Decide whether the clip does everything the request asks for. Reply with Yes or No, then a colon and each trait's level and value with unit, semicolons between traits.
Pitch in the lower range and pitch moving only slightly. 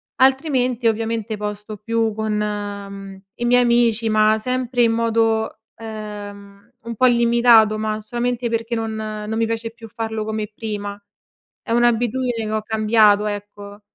No: high, 220 Hz; narrow, 1.8 semitones